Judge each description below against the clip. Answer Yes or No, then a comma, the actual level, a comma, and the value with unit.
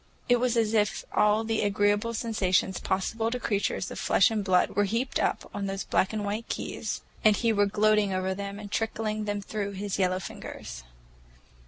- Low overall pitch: No, high, 205 Hz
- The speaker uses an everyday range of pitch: No, narrow, 2.0 semitones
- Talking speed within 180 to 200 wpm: Yes, average, 190 wpm